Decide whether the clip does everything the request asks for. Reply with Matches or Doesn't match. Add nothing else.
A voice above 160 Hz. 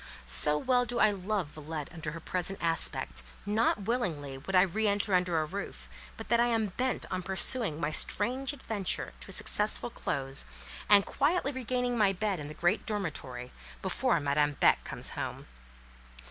Matches